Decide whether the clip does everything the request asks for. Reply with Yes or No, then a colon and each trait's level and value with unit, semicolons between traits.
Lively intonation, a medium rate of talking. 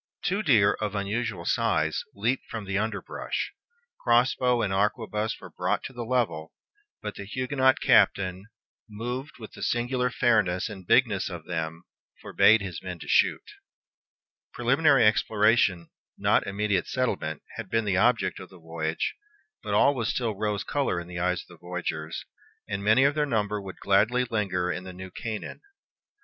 No: average, 4.5 semitones; average, 165 wpm